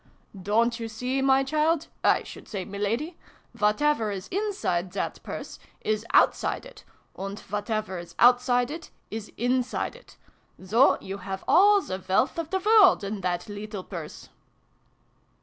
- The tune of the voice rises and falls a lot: Yes, wide, 6.8 semitones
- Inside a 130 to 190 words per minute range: Yes, average, 160 wpm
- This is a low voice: No, high, 225 Hz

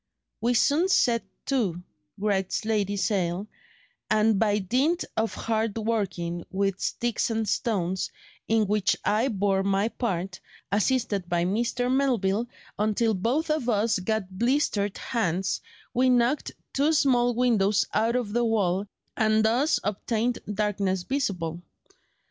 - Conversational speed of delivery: No, slow, 130 wpm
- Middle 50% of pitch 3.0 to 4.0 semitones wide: Yes, average, 3.7 semitones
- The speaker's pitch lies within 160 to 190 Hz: No, high, 215 Hz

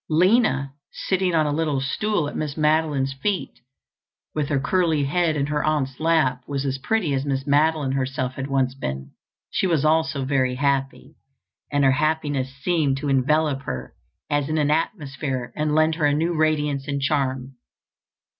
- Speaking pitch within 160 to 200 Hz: No, medium, 145 Hz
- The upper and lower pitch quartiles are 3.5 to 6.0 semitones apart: No, average, 2.7 semitones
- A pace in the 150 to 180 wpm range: Yes, average, 170 wpm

